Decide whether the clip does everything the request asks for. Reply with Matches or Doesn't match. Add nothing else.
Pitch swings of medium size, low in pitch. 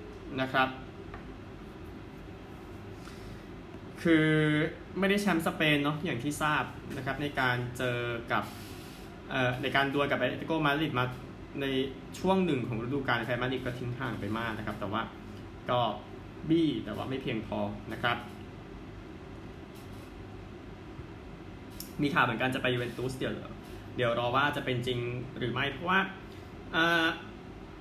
Matches